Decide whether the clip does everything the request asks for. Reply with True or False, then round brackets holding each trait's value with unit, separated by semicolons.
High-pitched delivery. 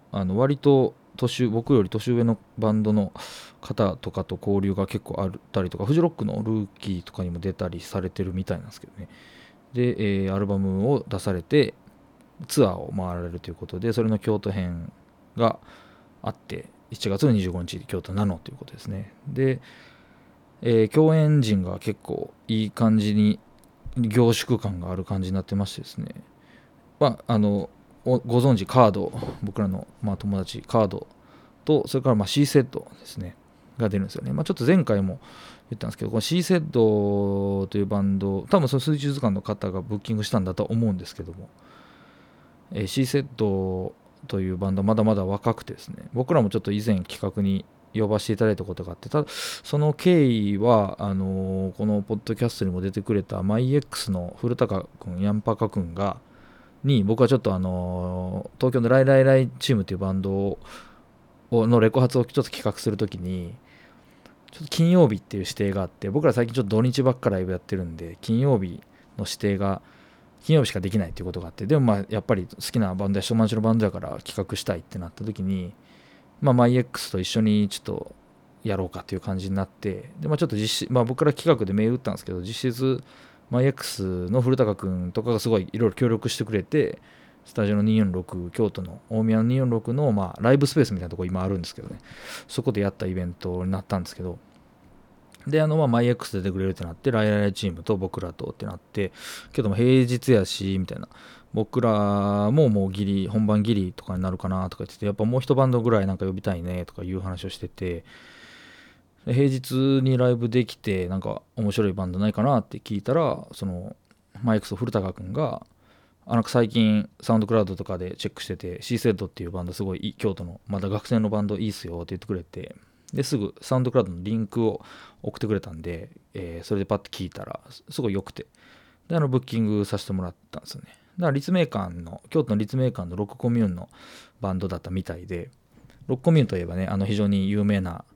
False (105 Hz)